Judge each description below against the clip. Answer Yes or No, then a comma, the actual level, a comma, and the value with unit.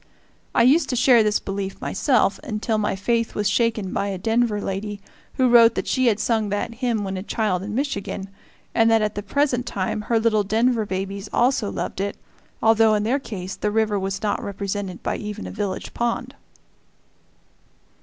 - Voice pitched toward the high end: Yes, high, 215 Hz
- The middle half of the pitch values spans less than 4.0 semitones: Yes, average, 2.7 semitones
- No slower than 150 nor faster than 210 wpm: Yes, average, 185 wpm